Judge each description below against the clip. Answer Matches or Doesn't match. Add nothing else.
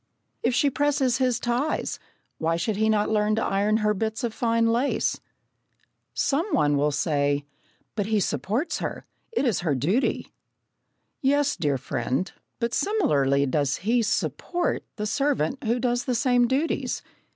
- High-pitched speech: Matches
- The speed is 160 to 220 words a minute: Doesn't match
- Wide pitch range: Matches